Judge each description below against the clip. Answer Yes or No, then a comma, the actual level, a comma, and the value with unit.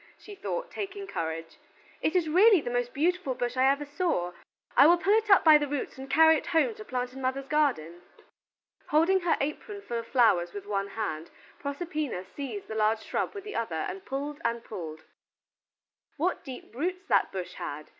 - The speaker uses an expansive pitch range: Yes, wide, 8.0 semitones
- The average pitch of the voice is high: Yes, very high, 275 Hz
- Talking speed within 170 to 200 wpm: Yes, average, 195 wpm